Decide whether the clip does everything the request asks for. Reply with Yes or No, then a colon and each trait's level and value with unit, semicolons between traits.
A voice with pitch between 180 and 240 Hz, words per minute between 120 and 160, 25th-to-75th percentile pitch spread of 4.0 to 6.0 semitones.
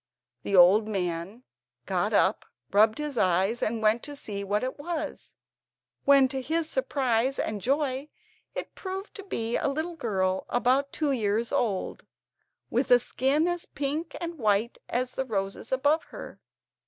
No: very high, 255 Hz; average, 155 wpm; wide, 5.4 semitones